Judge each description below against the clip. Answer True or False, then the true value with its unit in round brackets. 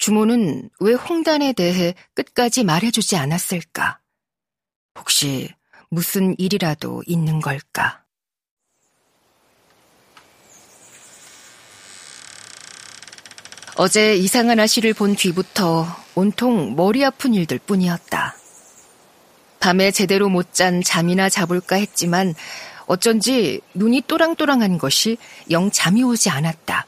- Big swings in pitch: False (4.9 semitones)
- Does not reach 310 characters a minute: True (205 characters per minute)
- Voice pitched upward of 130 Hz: True (190 Hz)